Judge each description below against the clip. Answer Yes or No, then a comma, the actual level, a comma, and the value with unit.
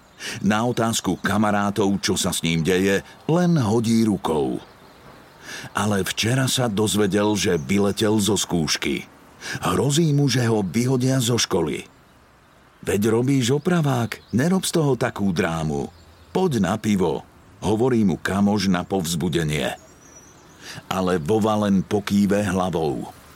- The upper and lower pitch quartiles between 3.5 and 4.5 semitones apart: Yes, average, 4.1 semitones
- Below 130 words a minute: Yes, average, 120 wpm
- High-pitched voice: No, low, 105 Hz